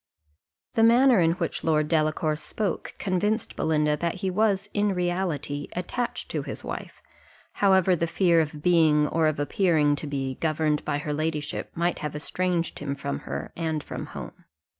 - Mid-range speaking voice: Yes, medium, 165 Hz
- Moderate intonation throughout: Yes, average, 3.6 semitones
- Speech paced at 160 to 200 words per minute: Yes, average, 165 wpm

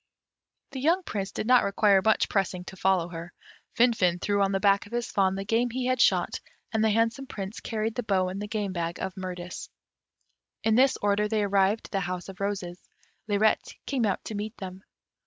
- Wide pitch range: No, average, 2.8 semitones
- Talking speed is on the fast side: Yes, fast, 210 wpm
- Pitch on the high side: Yes, high, 205 Hz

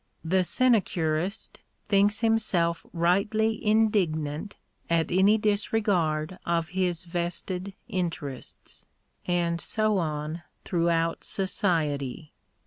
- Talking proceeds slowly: Yes, slow, 90 wpm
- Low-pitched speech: No, medium, 180 Hz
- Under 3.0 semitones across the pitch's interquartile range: No, average, 3.7 semitones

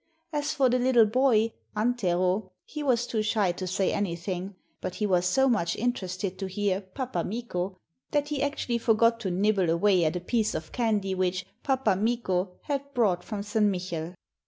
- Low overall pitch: No, high, 205 Hz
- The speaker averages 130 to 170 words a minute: No, average, 180 wpm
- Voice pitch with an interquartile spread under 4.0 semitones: No, average, 4.7 semitones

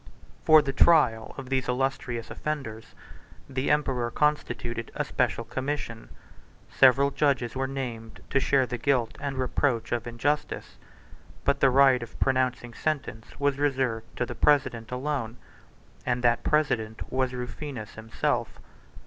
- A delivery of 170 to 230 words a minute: No, slow, 135 wpm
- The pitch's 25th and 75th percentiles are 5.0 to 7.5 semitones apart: No, average, 3.0 semitones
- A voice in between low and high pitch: No, low, 130 Hz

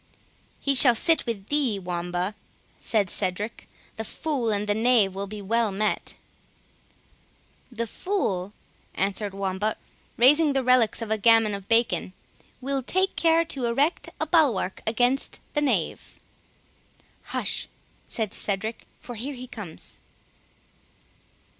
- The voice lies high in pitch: Yes, high, 225 Hz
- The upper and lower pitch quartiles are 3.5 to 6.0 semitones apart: Yes, average, 4.8 semitones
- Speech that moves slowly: Yes, slow, 130 wpm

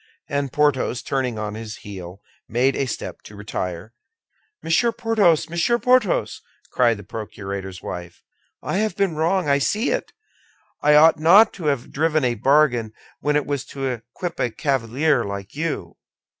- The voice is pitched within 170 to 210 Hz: No, medium, 140 Hz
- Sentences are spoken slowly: No, average, 155 wpm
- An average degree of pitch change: No, wide, 6.7 semitones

